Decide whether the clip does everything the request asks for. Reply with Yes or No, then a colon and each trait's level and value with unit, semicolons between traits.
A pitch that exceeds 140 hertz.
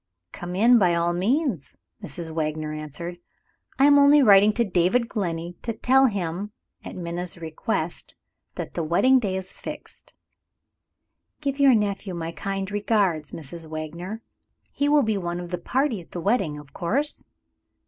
Yes: medium, 185 Hz